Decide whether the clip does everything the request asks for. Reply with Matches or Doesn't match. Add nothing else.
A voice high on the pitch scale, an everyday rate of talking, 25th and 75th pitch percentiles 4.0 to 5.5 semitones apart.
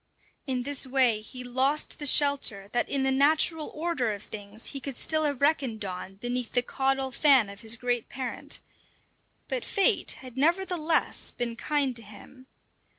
Doesn't match